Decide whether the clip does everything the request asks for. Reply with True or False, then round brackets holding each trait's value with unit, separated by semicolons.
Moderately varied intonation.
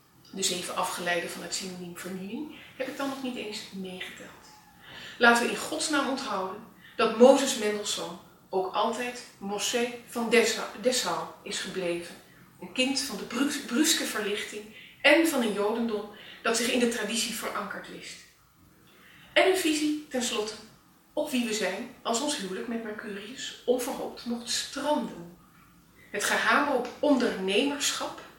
True (5.0 semitones)